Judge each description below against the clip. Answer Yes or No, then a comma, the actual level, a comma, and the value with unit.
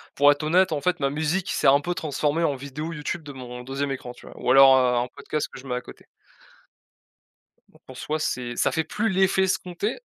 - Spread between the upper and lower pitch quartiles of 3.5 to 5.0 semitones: Yes, average, 4.0 semitones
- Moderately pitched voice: Yes, medium, 145 Hz